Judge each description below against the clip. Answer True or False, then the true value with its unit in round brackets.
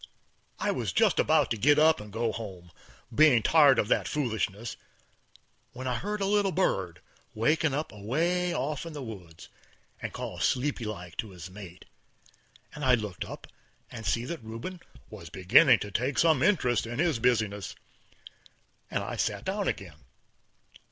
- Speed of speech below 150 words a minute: False (165 wpm)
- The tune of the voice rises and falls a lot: True (6.6 semitones)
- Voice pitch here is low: True (120 Hz)